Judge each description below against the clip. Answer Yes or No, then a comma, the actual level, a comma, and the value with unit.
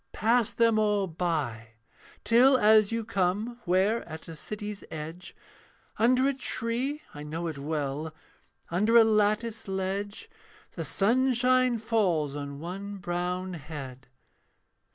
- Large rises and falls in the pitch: Yes, wide, 6.0 semitones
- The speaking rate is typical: No, slow, 125 wpm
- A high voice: Yes, high, 200 Hz